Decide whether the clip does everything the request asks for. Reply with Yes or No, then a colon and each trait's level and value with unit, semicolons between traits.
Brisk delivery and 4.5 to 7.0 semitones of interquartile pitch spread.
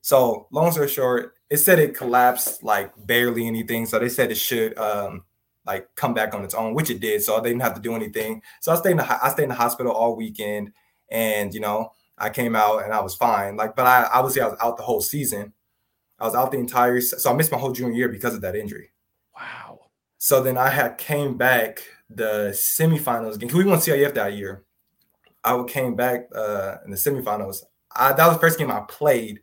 No: fast, 230 wpm; average, 3.8 semitones